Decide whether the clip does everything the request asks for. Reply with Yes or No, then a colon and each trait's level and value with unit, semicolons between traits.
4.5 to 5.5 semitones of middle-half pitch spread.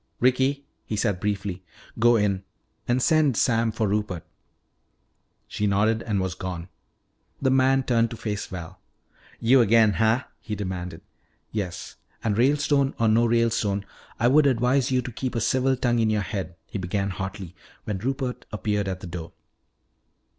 No: average, 4.0 semitones